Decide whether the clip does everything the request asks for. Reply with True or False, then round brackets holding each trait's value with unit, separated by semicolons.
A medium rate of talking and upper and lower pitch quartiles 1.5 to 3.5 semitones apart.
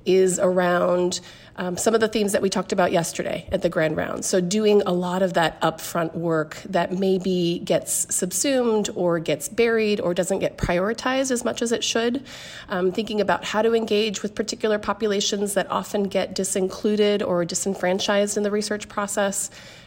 True (180 wpm; 2.9 semitones)